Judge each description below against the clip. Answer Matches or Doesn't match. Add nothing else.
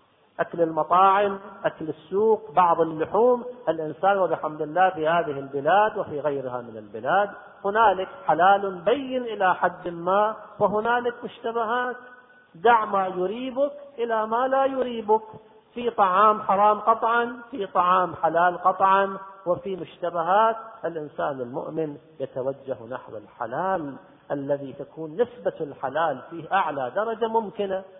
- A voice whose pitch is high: Matches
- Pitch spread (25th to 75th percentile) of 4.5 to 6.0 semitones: Matches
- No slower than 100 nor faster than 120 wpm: Matches